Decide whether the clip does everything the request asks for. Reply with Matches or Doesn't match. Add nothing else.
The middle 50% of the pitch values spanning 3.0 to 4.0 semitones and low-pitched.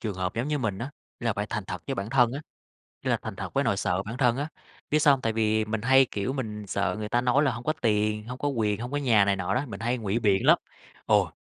Matches